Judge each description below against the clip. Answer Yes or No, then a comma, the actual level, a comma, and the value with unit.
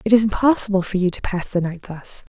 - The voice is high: Yes, high, 195 Hz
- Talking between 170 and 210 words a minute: No, fast, 255 wpm